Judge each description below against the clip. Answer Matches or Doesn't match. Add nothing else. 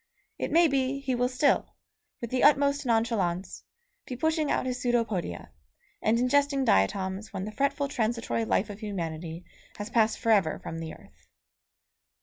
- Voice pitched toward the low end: Doesn't match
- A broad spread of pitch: Matches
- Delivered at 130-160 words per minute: Matches